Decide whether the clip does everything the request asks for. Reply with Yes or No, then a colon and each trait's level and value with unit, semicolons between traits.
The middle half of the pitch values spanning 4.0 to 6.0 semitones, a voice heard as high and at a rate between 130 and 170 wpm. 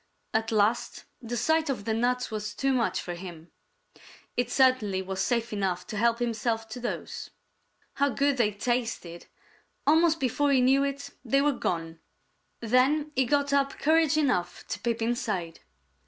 Yes: average, 4.6 semitones; high, 240 Hz; average, 160 wpm